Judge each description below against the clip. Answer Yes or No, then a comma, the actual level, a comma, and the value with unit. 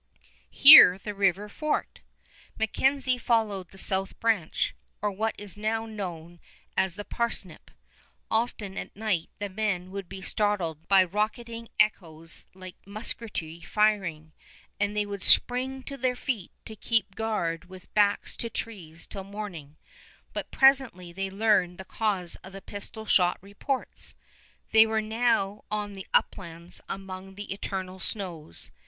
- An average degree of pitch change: Yes, average, 3.0 semitones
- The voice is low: No, high, 200 Hz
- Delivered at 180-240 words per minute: No, average, 140 wpm